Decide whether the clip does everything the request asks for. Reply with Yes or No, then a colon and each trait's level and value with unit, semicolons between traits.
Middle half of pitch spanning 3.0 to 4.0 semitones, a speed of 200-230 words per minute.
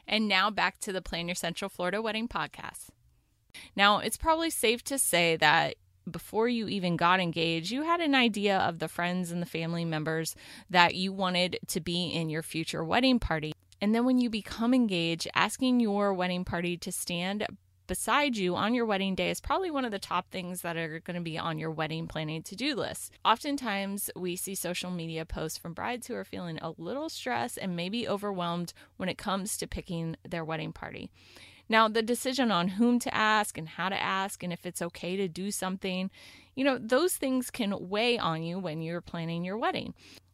No: average, 4.8 semitones; fast, 205 wpm